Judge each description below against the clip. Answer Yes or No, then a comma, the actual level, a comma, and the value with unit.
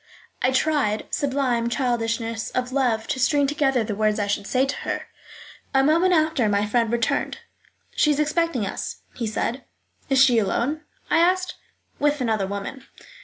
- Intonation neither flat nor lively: Yes, average, 4.5 semitones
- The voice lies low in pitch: No, very high, 255 Hz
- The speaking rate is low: No, average, 165 wpm